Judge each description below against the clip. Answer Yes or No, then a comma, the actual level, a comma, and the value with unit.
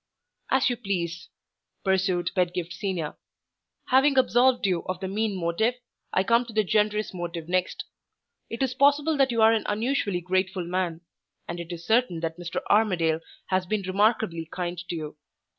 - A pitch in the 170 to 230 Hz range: Yes, high, 190 Hz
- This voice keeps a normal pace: Yes, average, 165 wpm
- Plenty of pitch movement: No, average, 4.4 semitones